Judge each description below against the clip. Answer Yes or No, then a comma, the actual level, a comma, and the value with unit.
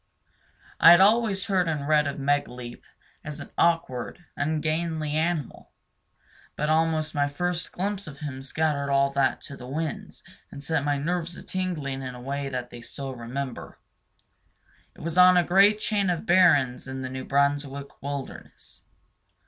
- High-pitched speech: No, medium, 150 Hz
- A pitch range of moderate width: Yes, average, 3.8 semitones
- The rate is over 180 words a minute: No, average, 160 wpm